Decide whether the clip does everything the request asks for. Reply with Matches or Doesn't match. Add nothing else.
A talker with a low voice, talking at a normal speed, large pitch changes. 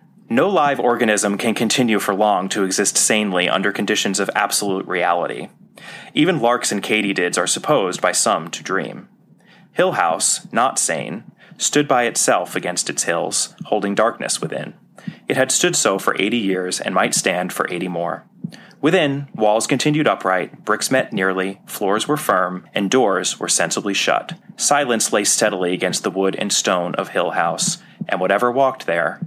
Doesn't match